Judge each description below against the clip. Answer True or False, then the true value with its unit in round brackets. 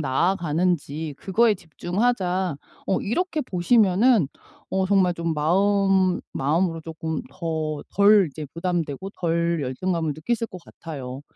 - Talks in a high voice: False (175 Hz)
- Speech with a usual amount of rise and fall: True (3.5 semitones)